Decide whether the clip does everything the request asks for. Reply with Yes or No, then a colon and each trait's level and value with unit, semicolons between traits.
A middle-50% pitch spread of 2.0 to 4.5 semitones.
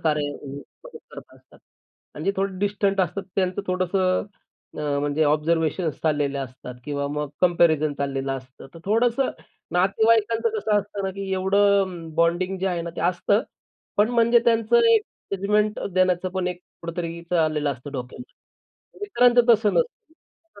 No: average, 4.9 semitones